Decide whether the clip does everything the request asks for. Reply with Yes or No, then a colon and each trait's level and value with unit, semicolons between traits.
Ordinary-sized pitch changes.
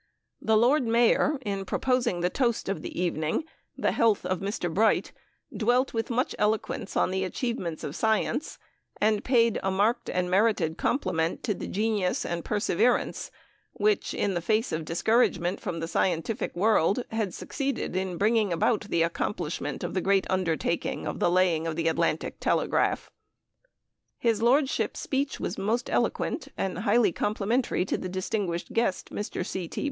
Yes: average, 4.5 semitones